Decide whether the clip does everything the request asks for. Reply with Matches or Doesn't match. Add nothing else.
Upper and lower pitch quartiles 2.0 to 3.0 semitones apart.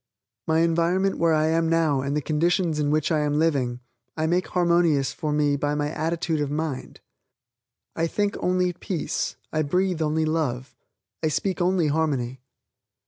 Matches